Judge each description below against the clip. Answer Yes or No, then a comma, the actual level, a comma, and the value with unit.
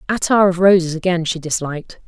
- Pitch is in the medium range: Yes, medium, 175 Hz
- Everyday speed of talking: Yes, average, 175 wpm